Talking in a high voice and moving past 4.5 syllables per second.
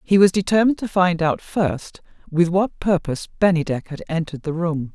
No: medium, 175 Hz; 5.4 syllables/s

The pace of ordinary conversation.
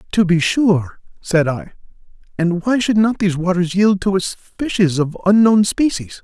Yes: average, 175 wpm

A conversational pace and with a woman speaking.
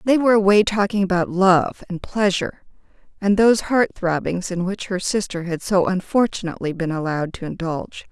Yes: average, 170 wpm; female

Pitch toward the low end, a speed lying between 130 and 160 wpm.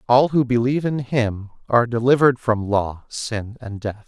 No: low, 120 Hz; average, 175 wpm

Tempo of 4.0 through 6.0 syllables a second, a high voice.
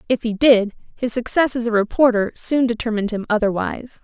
Yes: 5.8 syllables/s; high, 230 Hz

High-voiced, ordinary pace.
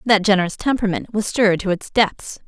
Yes: high, 200 Hz; average, 195 wpm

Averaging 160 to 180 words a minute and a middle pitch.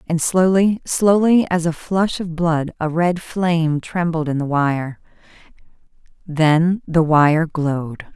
No: average, 140 wpm; medium, 165 Hz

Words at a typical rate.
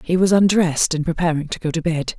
No: fast, 245 wpm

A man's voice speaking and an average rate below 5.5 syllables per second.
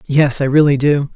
Yes: male; 5.0 syllables/s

